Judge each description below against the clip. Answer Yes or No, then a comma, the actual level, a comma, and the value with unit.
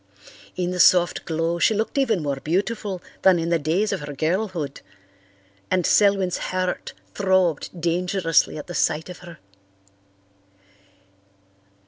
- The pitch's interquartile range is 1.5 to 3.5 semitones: Yes, narrow, 2.6 semitones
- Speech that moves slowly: Yes, slow, 125 wpm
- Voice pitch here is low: No, medium, 180 Hz